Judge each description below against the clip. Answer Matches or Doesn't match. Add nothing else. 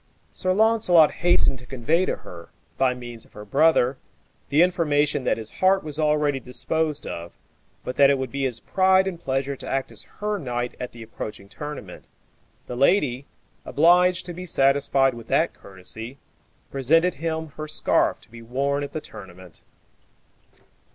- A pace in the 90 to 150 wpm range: Doesn't match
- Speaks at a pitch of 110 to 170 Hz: Matches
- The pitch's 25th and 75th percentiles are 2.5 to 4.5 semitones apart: Doesn't match